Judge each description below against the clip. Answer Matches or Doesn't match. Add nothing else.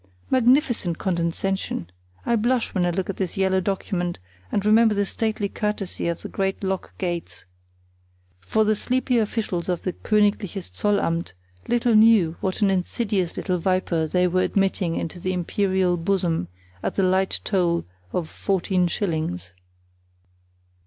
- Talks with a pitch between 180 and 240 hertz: Matches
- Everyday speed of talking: Matches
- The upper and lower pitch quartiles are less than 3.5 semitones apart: Matches